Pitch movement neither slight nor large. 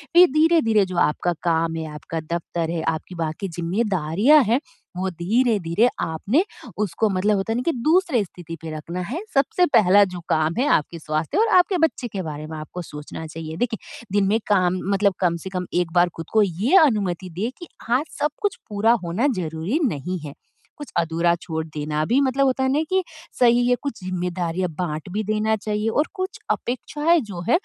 No: wide, 6.5 semitones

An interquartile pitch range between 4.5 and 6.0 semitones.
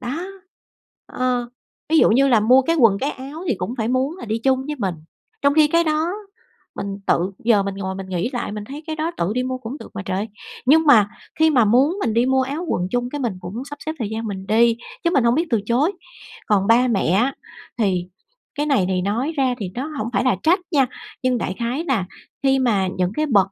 Yes: average, 5.2 semitones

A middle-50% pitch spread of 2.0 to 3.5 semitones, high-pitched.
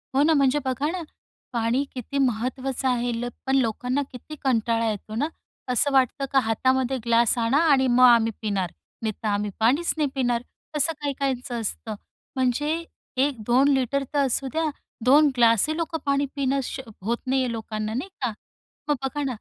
Yes: average, 3.2 semitones; very high, 255 Hz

